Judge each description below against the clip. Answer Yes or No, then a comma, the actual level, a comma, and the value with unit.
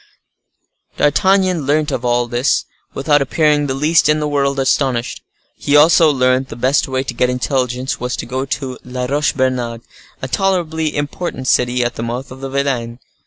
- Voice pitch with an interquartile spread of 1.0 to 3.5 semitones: Yes, average, 2.8 semitones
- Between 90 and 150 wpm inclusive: No, average, 170 wpm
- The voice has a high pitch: No, low, 135 Hz